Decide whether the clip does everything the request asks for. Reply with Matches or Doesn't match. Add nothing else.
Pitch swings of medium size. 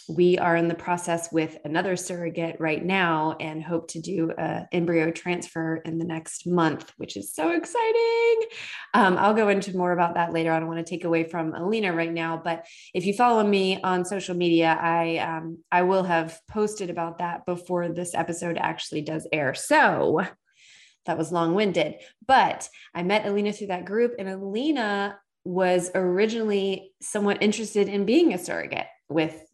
Matches